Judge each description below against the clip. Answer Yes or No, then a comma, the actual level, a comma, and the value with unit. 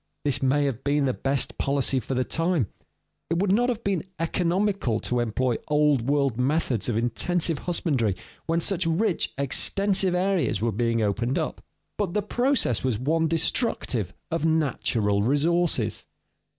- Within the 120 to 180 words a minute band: Yes, average, 150 wpm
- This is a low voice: No, medium, 145 Hz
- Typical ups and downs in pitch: No, wide, 6.1 semitones